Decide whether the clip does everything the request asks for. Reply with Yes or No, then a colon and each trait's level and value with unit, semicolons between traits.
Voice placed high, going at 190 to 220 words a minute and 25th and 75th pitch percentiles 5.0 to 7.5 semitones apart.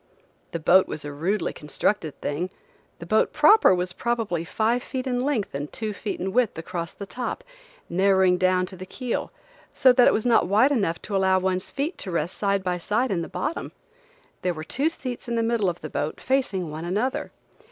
Yes: high, 195 Hz; fast, 205 wpm; average, 5.3 semitones